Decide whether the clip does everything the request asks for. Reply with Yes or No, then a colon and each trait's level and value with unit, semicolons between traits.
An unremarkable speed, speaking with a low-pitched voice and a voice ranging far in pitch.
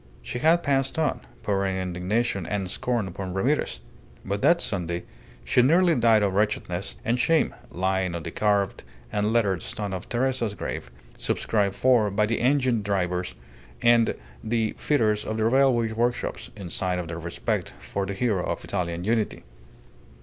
No: average, 160 wpm; low, 105 Hz; average, 4.2 semitones